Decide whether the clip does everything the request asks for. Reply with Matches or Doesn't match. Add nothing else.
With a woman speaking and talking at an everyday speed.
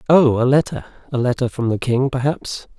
Doesn't match